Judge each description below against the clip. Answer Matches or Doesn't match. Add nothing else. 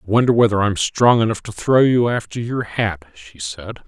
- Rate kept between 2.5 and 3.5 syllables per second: Doesn't match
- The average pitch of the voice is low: Matches